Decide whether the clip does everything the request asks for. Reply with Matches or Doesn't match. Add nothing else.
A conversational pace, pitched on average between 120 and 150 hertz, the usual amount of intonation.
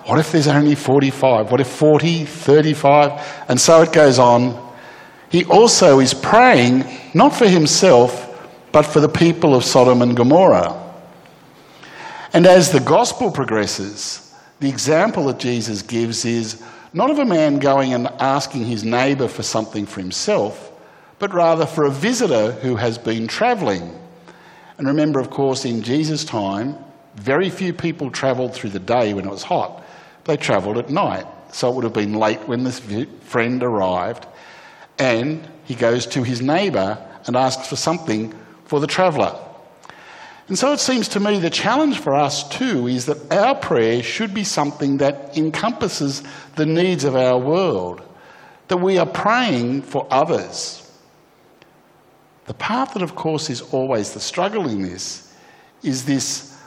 Matches